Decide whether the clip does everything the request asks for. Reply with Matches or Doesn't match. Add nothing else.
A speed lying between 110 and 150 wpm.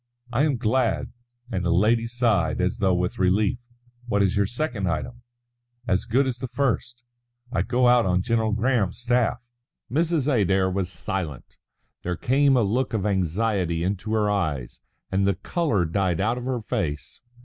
Doesn't match